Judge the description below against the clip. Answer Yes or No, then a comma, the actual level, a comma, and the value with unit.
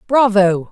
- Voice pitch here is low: No, high, 205 Hz